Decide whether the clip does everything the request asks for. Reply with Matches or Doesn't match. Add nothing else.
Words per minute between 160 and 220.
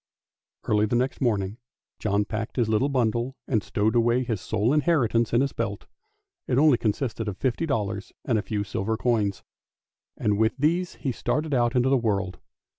Matches